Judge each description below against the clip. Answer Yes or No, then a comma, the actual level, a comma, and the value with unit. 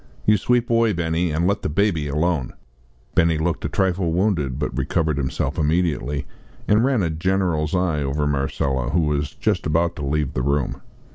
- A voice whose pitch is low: Yes, very low, 80 Hz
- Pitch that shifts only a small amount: No, average, 3.7 semitones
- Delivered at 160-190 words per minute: Yes, average, 180 wpm